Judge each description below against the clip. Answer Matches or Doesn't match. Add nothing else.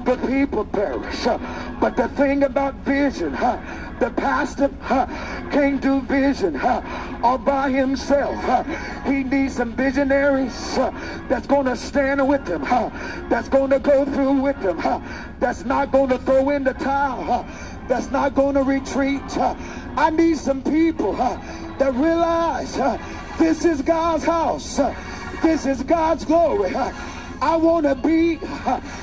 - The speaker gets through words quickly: Doesn't match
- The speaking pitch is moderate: Doesn't match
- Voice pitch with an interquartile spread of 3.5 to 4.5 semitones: Doesn't match